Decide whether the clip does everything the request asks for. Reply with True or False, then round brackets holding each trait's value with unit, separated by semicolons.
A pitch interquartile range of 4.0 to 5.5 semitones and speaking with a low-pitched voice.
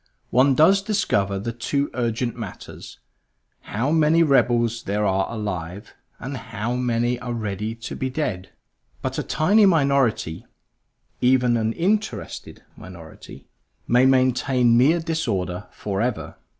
True (4.7 semitones; 120 Hz)